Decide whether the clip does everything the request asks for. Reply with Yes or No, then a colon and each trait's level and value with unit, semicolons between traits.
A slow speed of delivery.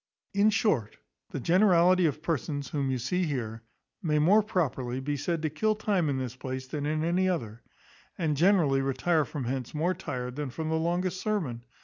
No: average, 190 wpm